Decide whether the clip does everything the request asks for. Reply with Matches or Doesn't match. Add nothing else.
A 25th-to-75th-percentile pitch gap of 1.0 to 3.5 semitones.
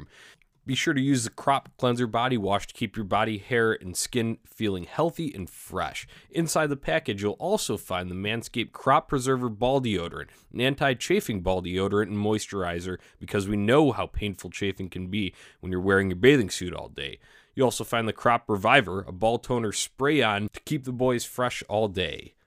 Doesn't match